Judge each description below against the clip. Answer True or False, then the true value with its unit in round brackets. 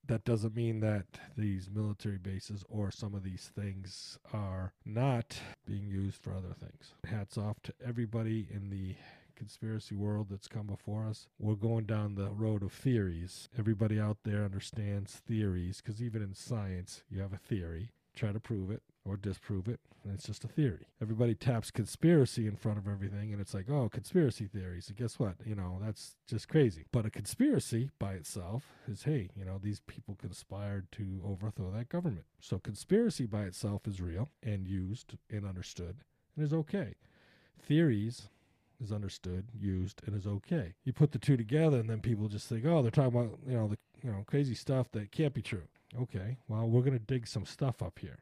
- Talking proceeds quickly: False (195 wpm)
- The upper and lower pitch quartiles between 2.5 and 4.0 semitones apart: True (3.4 semitones)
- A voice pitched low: True (110 Hz)